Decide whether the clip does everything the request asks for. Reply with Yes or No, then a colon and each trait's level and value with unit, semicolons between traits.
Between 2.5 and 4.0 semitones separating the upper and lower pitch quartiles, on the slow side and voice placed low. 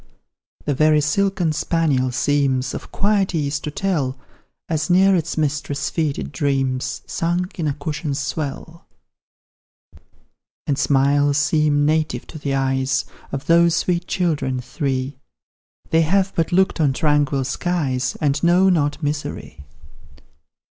No: average, 3.4 semitones; slow, 130 wpm; medium, 150 Hz